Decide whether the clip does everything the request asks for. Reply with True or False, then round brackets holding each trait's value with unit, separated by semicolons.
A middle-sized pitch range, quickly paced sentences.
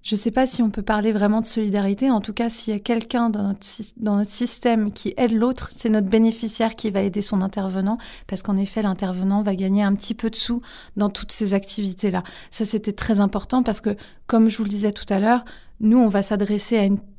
False (2.2 semitones; 240 wpm)